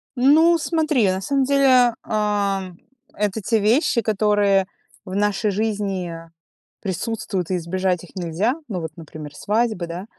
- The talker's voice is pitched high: Yes, high, 205 Hz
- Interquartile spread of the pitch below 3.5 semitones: No, average, 3.8 semitones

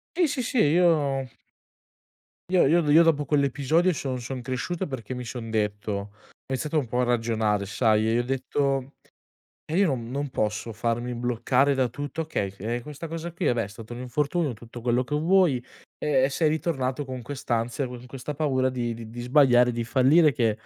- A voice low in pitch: Yes, low, 130 Hz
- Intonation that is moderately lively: Yes, average, 3.9 semitones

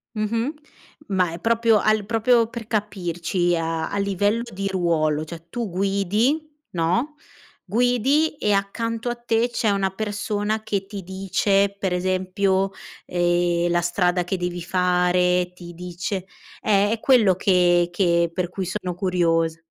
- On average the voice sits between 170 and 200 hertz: Yes, high, 190 Hz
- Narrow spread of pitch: No, average, 3.4 semitones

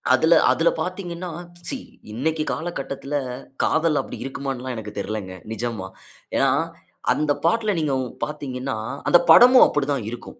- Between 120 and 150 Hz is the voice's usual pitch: Yes, medium, 140 Hz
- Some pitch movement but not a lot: No, wide, 5.7 semitones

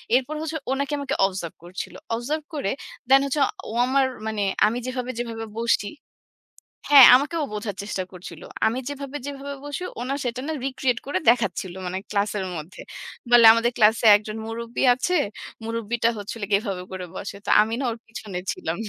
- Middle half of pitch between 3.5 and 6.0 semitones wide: Yes, average, 4.7 semitones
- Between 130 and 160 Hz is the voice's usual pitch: No, high, 230 Hz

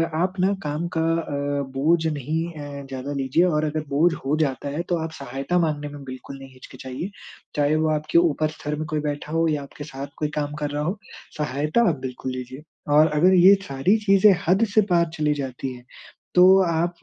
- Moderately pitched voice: Yes, medium, 150 Hz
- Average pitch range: Yes, average, 3.2 semitones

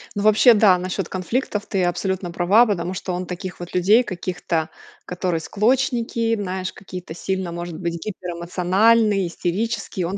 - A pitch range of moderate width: Yes, average, 3.1 semitones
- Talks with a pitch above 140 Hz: Yes, medium, 185 Hz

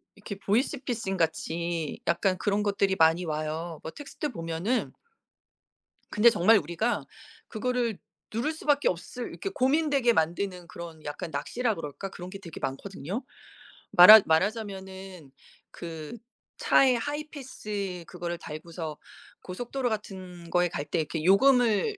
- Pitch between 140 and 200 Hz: Yes, high, 190 Hz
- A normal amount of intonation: No, wide, 5.9 semitones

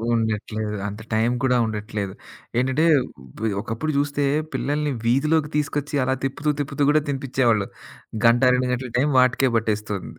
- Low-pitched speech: Yes, low, 130 Hz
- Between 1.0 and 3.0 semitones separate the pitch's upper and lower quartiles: No, average, 4.5 semitones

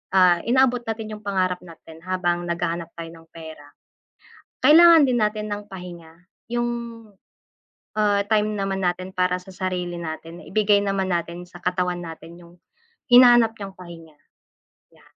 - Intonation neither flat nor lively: Yes, average, 3.6 semitones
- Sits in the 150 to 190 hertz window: Yes, medium, 185 Hz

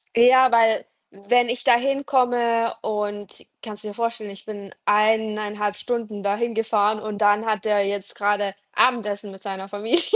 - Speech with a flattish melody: Yes, narrow, 2.2 semitones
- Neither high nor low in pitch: No, high, 215 Hz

